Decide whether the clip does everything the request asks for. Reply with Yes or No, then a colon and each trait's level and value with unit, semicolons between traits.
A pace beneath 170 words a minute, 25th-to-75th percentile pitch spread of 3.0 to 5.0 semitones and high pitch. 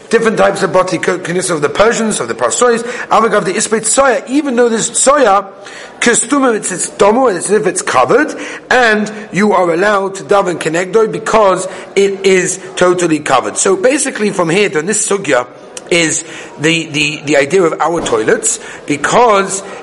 Yes: average, 160 wpm; average, 4.0 semitones; high, 195 Hz